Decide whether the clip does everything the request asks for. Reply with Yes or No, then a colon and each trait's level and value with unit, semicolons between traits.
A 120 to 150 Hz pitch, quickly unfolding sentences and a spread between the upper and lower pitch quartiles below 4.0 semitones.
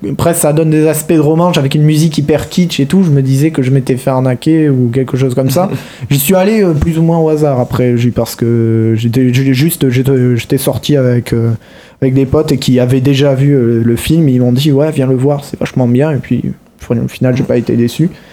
Yes: low, 135 Hz; fast, 230 wpm; average, 3.6 semitones